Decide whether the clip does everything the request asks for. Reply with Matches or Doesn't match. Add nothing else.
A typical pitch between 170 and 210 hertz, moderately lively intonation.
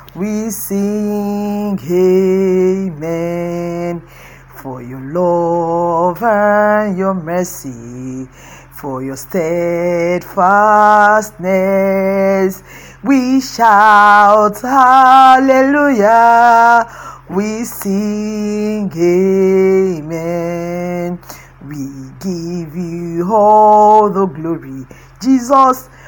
Matches